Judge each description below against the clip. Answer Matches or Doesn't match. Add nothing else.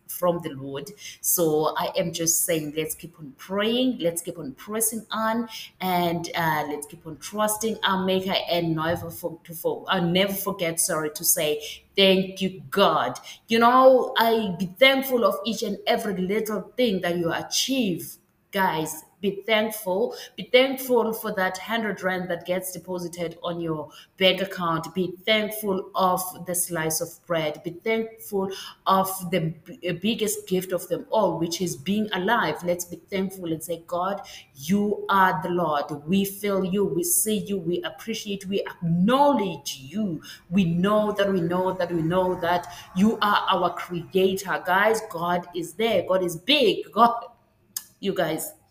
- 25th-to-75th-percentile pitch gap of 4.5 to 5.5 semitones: Doesn't match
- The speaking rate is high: Doesn't match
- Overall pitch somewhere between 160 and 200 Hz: Matches